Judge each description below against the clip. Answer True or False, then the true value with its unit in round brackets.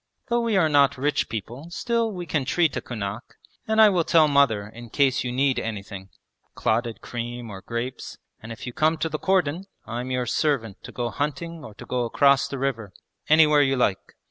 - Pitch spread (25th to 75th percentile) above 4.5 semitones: True (5.0 semitones)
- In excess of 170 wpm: True (200 wpm)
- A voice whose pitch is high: False (135 Hz)